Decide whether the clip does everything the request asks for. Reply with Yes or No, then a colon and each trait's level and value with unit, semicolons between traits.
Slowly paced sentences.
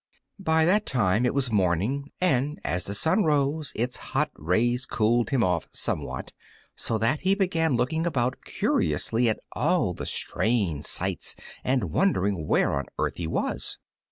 No: average, 155 wpm